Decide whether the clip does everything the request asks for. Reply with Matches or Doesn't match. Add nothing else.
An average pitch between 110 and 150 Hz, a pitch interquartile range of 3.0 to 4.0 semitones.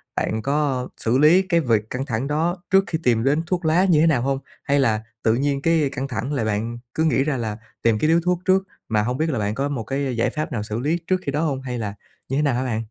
Doesn't match